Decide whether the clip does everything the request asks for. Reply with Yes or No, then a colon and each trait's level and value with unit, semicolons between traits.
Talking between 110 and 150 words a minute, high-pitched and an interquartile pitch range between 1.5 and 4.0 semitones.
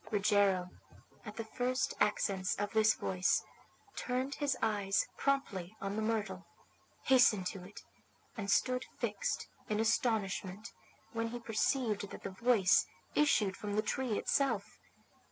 Yes: slow, 135 wpm; high, 215 Hz; average, 3.4 semitones